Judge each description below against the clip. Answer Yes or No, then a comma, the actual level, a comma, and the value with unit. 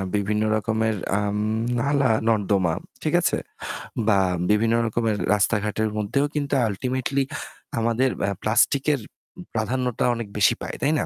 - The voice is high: No, low, 110 Hz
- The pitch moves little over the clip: No, average, 3.5 semitones